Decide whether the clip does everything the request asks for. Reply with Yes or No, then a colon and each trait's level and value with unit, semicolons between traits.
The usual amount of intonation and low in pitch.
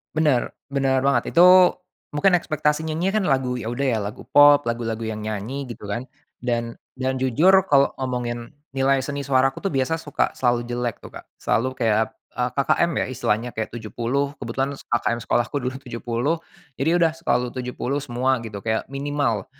Yes: average, 3.2 semitones; low, 130 Hz